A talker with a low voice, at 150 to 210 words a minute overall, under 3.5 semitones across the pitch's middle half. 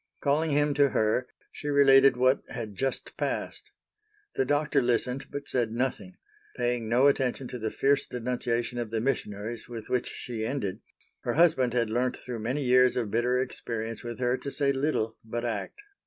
Yes: low, 125 Hz; average, 175 wpm; average, 2.8 semitones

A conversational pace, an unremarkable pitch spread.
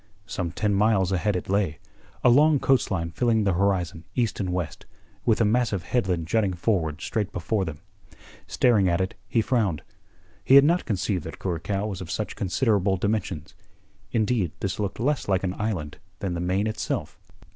Yes: average, 180 wpm; average, 3.7 semitones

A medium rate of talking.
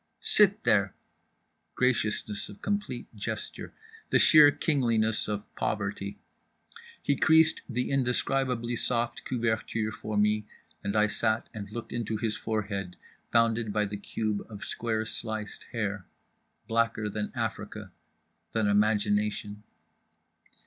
No: slow, 115 wpm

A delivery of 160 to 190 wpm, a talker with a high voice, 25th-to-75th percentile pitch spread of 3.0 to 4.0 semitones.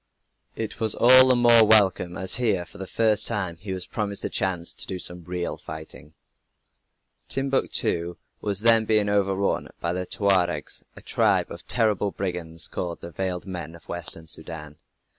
No: average, 165 wpm; very low, 95 Hz; average, 3.7 semitones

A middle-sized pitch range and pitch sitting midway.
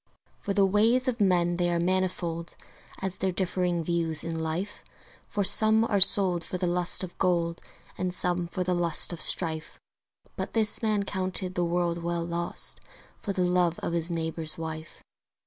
No: narrow, 2.0 semitones; medium, 175 Hz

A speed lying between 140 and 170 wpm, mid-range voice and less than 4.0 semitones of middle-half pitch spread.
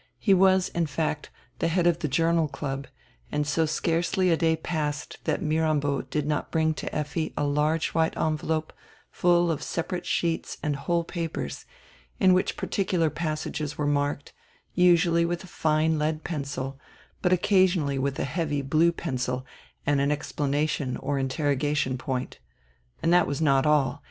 Yes: average, 160 wpm; medium, 155 Hz; average, 2.7 semitones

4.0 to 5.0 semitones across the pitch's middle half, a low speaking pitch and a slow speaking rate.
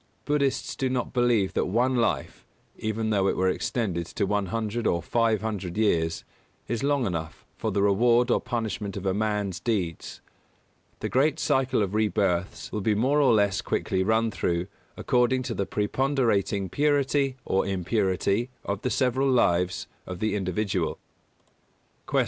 No: average, 4.3 semitones; low, 110 Hz; average, 160 wpm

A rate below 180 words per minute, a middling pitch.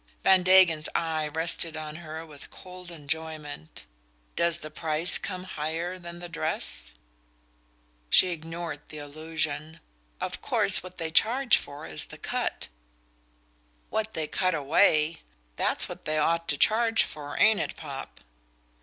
Yes: average, 145 wpm; medium, 160 Hz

